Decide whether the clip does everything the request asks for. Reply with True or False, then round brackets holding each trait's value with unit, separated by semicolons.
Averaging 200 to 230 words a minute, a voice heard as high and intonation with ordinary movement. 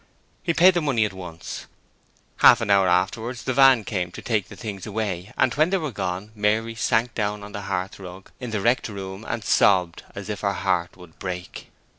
False (205 wpm; 105 Hz; 3.4 semitones)